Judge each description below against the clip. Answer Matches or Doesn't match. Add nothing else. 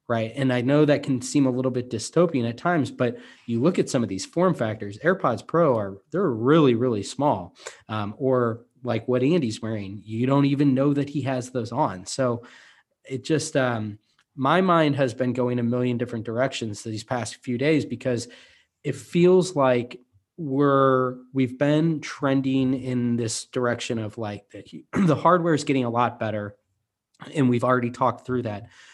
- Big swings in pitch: Doesn't match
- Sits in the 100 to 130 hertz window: Matches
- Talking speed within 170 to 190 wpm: Matches